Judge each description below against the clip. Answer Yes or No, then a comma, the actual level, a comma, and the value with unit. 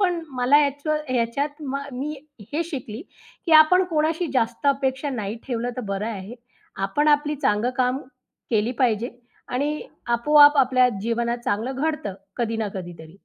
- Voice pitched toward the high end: Yes, very high, 255 Hz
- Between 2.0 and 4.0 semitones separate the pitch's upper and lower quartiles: No, average, 4.4 semitones